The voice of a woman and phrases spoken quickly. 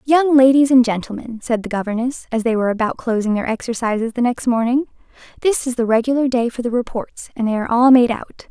Yes: female; fast, 220 wpm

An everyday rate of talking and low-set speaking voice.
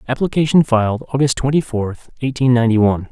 Yes: average, 155 wpm; low, 125 Hz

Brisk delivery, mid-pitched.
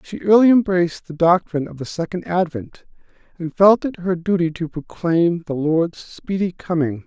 No: average, 170 wpm; medium, 170 Hz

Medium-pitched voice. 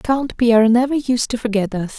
No: high, 235 Hz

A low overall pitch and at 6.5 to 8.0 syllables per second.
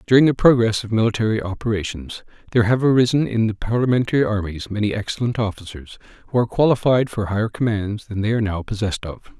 Yes: low, 110 Hz; 6.6 syllables/s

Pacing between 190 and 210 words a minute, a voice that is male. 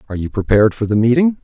No: fast, 250 wpm; male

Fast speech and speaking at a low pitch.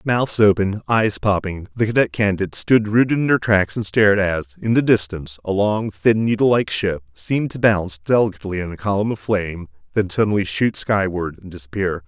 No: average, 190 wpm; low, 100 Hz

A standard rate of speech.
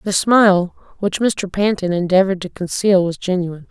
Yes: average, 160 wpm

